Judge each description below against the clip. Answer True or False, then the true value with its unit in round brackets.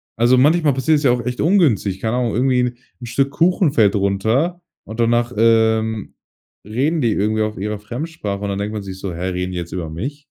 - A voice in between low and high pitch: False (115 Hz)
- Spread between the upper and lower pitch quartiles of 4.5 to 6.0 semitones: True (4.9 semitones)